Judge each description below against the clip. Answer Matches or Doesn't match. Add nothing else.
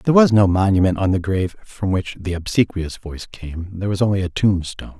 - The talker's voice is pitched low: Matches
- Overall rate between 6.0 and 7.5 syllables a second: Matches